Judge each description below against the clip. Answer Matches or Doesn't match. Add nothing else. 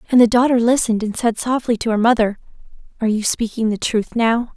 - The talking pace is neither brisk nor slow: Doesn't match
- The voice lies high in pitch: Matches